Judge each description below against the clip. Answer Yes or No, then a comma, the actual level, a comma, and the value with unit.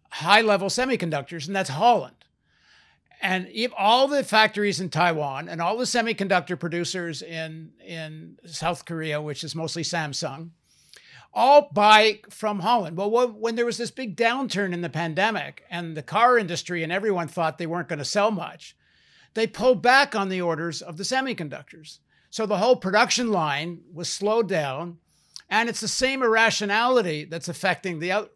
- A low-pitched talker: No, high, 190 Hz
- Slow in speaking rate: No, average, 165 wpm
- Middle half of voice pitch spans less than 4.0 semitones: No, average, 5.2 semitones